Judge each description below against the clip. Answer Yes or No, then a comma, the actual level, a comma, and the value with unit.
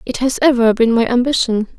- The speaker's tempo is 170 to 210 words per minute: Yes, average, 200 wpm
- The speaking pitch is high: Yes, high, 240 Hz